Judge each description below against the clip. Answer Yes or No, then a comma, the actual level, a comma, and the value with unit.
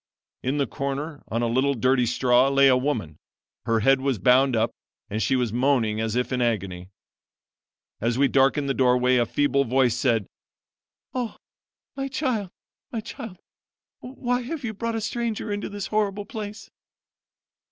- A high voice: No, low, 135 Hz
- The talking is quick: No, average, 165 wpm